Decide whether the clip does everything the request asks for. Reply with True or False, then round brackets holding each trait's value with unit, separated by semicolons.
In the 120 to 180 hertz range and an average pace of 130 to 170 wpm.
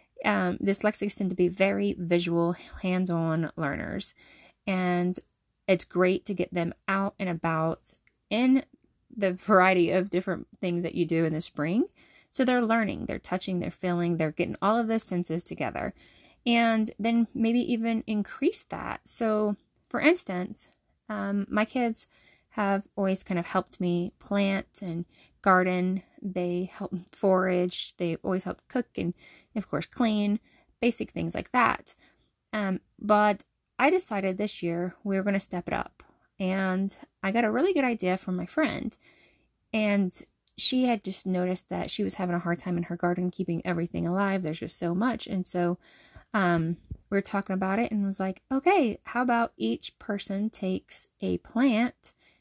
False (190 Hz; 165 wpm)